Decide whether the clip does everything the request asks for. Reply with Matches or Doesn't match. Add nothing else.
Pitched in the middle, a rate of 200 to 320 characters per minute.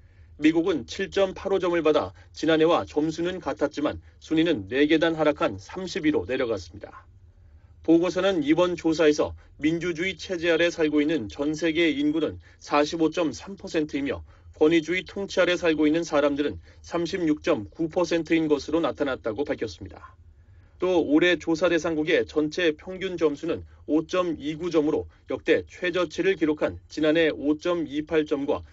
Matches